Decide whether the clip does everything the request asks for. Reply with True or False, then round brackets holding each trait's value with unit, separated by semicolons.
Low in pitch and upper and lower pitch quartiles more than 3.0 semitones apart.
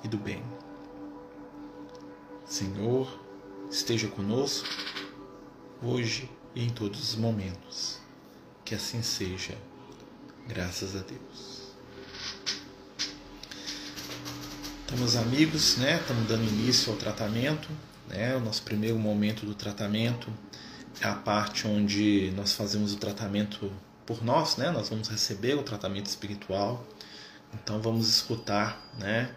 False (105 Hz; 2.6 semitones)